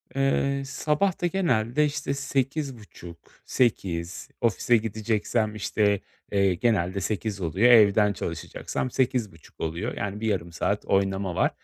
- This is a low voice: Yes, low, 110 Hz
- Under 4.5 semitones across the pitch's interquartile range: No, average, 4.9 semitones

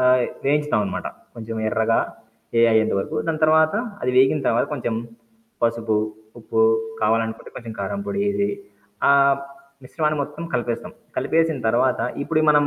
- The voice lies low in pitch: Yes, low, 130 Hz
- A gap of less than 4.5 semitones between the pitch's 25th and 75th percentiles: No, wide, 5.4 semitones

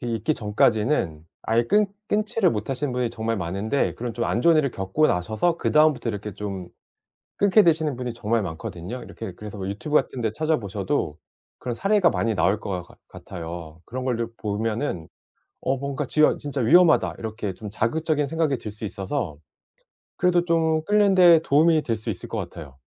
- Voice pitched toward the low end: Yes, low, 115 Hz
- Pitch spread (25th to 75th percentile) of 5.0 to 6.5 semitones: No, wide, 6.9 semitones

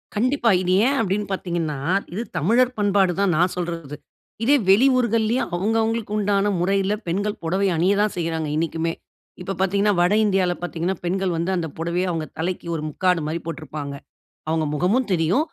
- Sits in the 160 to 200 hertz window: Yes, medium, 185 Hz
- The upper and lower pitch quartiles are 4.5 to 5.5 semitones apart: No, average, 3.8 semitones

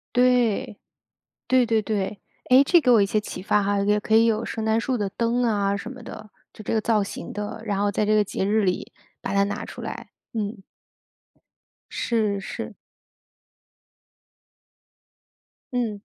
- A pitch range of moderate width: No, narrow, 2.3 semitones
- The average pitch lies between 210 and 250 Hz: Yes, high, 215 Hz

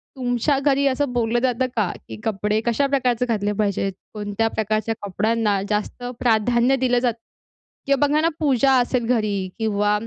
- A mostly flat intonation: No, average, 3.4 semitones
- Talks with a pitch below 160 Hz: No, high, 235 Hz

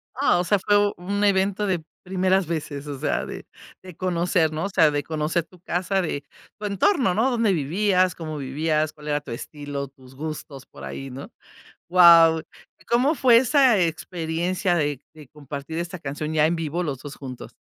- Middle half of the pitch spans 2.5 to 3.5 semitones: No, average, 4.2 semitones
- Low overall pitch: No, medium, 165 Hz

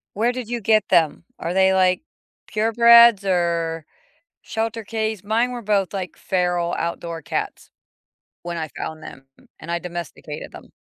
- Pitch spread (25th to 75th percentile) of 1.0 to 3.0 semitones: No, average, 4.5 semitones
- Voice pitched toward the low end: No, high, 190 Hz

